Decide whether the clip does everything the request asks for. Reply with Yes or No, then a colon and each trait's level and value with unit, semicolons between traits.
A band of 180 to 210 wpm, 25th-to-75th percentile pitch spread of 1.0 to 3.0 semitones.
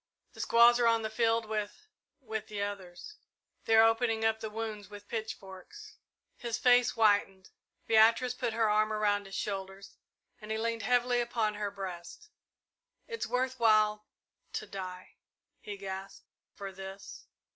No: average, 155 wpm; narrow, 2.4 semitones